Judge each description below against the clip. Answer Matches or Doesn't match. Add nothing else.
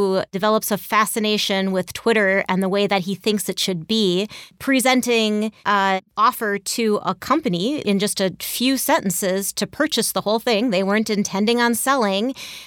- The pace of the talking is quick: Doesn't match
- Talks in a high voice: Matches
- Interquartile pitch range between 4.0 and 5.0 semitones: Doesn't match